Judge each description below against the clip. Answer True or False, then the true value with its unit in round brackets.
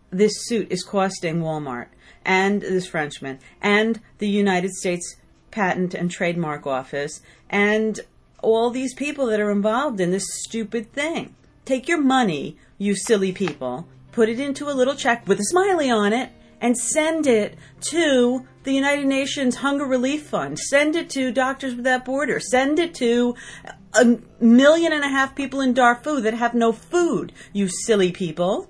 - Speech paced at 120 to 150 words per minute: False (165 wpm)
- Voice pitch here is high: True (230 Hz)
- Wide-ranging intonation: True (6.0 semitones)